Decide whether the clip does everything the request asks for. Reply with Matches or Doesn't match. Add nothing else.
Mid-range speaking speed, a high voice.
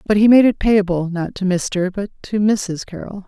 Doesn't match